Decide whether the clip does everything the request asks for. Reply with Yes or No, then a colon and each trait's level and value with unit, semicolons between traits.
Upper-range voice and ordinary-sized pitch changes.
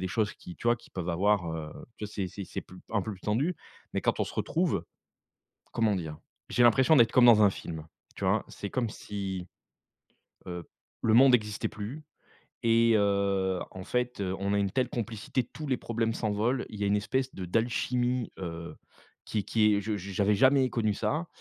No: low, 105 Hz; average, 3.6 semitones